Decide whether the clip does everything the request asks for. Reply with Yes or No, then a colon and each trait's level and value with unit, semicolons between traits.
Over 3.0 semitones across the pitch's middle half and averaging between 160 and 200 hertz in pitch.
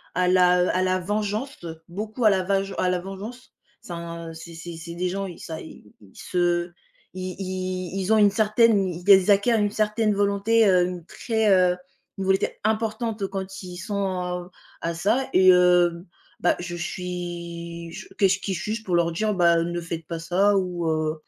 No: average, 2.7 semitones; medium, 185 Hz